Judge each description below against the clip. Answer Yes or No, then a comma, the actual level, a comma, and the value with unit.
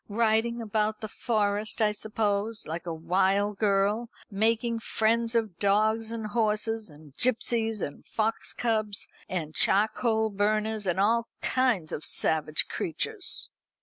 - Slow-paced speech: Yes, slow, 130 wpm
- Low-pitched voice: No, high, 215 Hz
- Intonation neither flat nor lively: No, narrow, 2.2 semitones